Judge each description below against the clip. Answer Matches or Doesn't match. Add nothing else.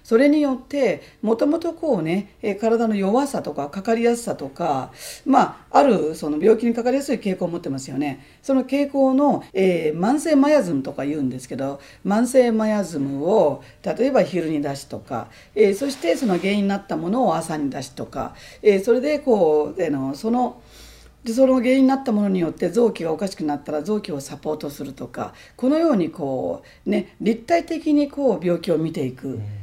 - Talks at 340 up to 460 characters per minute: Matches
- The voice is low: Doesn't match